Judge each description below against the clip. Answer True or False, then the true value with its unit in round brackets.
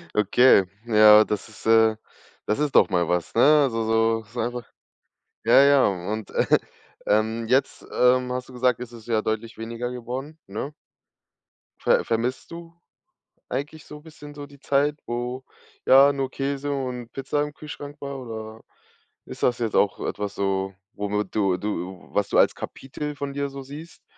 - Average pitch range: True (4.3 semitones)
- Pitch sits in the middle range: False (120 Hz)